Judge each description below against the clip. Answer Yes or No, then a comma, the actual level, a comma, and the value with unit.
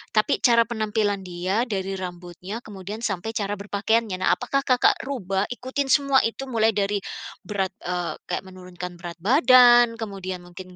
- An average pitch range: Yes, average, 4.1 semitones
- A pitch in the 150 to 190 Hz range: No, high, 200 Hz